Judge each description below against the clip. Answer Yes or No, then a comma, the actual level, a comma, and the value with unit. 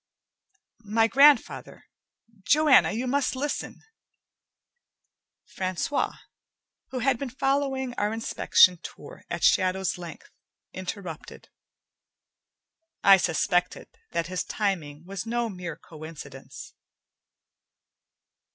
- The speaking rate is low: Yes, slow, 90 wpm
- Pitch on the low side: No, high, 200 Hz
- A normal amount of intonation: No, wide, 6.6 semitones